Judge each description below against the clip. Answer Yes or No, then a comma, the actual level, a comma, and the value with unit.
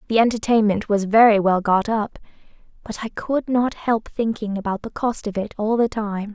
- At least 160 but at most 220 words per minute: Yes, average, 200 wpm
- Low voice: No, high, 215 Hz